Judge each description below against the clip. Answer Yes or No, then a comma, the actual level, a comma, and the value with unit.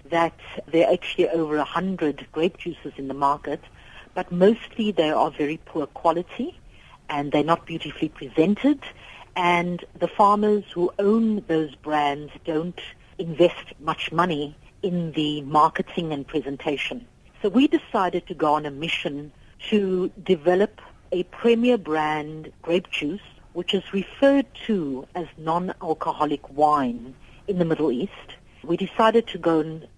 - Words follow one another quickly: No, average, 140 wpm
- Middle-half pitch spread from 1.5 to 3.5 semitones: No, average, 4.1 semitones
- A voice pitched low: No, medium, 170 Hz